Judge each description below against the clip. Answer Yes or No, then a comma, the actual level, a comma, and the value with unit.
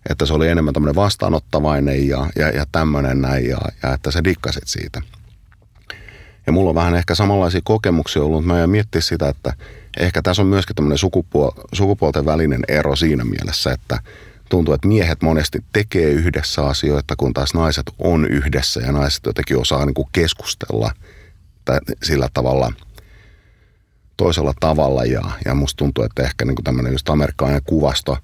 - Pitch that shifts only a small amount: No, average, 4.1 semitones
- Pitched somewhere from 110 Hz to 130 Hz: No, very low, 80 Hz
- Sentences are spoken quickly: Yes, fast, 170 wpm